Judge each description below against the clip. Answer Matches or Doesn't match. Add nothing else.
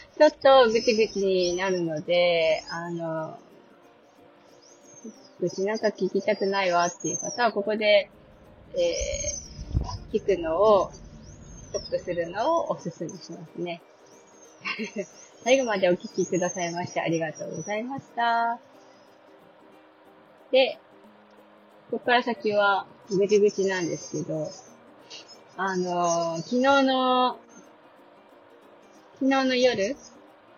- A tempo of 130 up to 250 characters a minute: Matches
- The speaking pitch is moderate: Doesn't match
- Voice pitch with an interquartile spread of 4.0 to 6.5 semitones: Matches